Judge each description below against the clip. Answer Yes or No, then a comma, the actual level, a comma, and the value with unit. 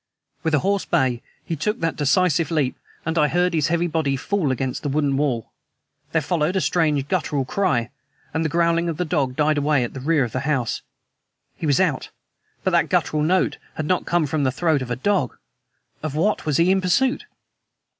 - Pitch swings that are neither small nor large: Yes, average, 3.7 semitones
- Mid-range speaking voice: Yes, medium, 155 Hz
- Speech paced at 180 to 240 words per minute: Yes, fast, 205 wpm